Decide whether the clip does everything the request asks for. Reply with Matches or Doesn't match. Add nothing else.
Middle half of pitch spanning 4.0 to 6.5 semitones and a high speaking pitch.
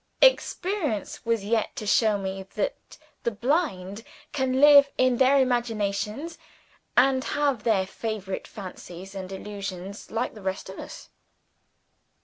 Matches